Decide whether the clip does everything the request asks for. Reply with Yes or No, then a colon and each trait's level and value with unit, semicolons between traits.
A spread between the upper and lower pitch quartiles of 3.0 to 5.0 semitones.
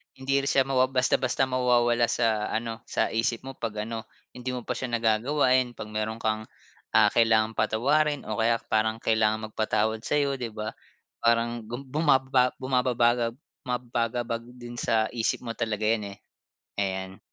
No: narrow, 2.4 semitones